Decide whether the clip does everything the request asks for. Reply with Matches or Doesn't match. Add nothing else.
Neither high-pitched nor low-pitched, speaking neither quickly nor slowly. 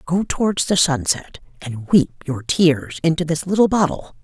Matches